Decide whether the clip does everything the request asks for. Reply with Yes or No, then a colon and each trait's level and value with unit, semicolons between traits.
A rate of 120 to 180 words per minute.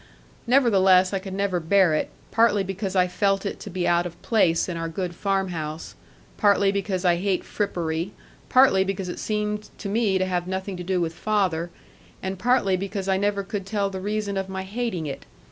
No: average, 200 wpm